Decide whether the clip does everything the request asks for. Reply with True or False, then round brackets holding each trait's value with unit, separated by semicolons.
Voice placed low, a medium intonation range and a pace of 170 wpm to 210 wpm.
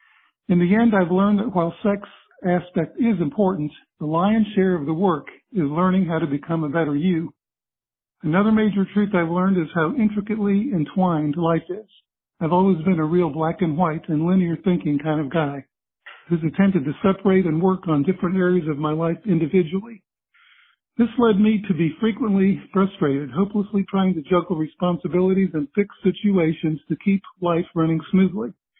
False (180 Hz; 3.5 semitones; 175 wpm)